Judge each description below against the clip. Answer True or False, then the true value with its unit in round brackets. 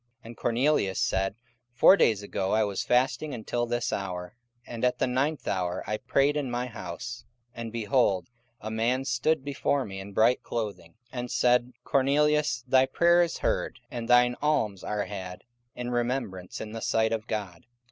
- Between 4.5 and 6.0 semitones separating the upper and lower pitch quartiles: False (4.1 semitones)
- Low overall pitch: True (120 Hz)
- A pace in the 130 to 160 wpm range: False (180 wpm)